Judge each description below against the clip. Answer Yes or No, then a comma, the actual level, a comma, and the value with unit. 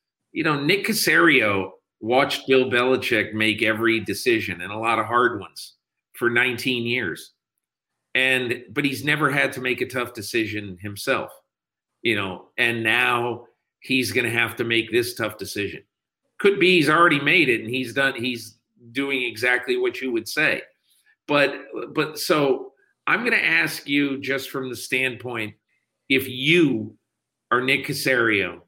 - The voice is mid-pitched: No, low, 130 Hz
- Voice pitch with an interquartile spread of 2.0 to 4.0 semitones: Yes, average, 3.4 semitones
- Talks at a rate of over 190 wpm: No, average, 160 wpm